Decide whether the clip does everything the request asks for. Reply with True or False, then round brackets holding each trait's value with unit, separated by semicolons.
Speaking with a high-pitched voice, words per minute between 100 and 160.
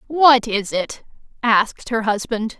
True (230 Hz; 140 wpm)